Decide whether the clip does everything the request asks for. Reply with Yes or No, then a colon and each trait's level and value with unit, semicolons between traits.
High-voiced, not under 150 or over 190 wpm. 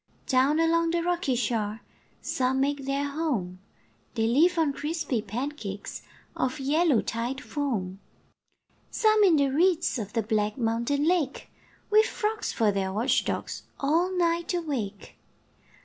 No: very high, 275 Hz; slow, 135 wpm